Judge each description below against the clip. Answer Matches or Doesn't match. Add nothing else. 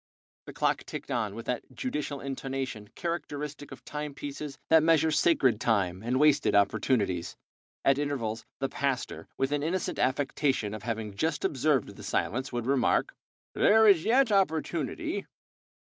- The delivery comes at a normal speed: Matches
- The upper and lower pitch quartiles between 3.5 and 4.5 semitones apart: Matches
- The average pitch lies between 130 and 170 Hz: Matches